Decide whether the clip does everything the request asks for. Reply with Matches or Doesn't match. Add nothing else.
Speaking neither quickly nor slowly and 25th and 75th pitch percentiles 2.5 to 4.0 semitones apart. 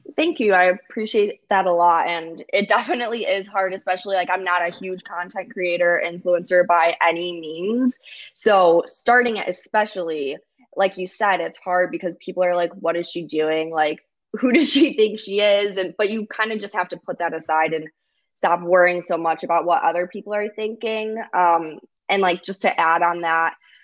Matches